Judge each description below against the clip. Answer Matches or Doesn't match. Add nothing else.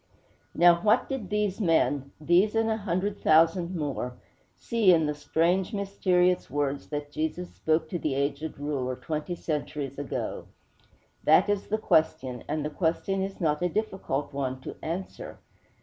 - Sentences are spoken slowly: Doesn't match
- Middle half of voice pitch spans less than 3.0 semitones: Doesn't match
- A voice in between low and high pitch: Matches